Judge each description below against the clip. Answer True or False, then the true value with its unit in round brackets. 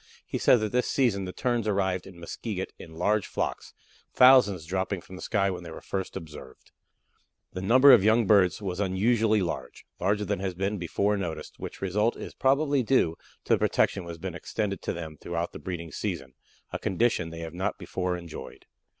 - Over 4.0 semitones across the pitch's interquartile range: False (3.6 semitones)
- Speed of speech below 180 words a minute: False (195 wpm)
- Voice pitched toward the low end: True (95 Hz)